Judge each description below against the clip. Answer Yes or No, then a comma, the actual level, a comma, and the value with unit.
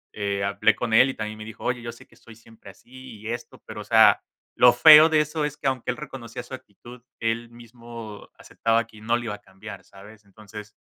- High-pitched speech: No, low, 115 Hz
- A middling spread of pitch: No, narrow, 2.3 semitones